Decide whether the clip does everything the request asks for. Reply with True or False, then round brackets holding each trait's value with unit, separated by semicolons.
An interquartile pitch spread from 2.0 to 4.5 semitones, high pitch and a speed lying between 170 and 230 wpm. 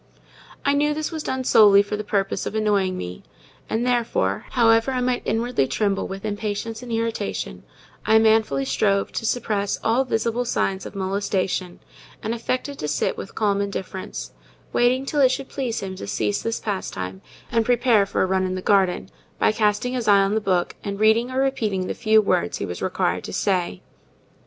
True (3.6 semitones; 215 Hz; 190 wpm)